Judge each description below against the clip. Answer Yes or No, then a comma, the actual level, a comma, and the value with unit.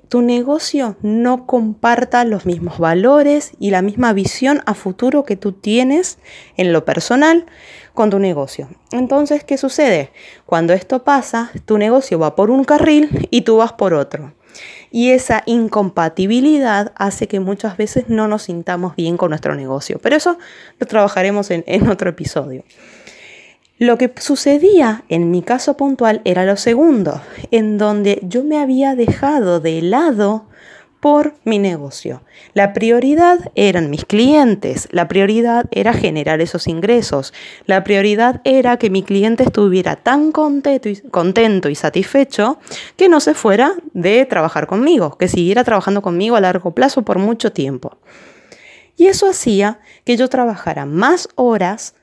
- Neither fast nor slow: Yes, average, 150 wpm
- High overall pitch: Yes, high, 220 Hz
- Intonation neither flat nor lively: No, wide, 5.9 semitones